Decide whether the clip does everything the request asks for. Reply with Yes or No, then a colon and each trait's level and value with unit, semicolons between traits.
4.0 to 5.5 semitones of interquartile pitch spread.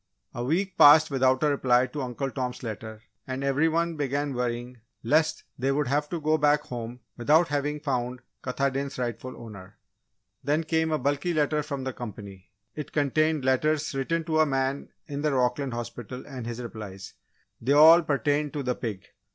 No: average, 3.4 semitones